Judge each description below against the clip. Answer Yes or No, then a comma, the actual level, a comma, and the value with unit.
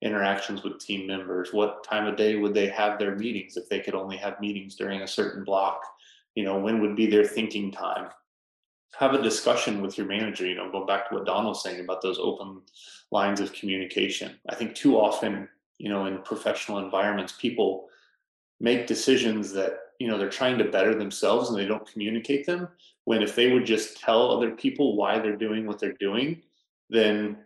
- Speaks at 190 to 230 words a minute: Yes, average, 200 wpm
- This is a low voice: Yes, low, 105 Hz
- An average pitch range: No, narrow, 2.1 semitones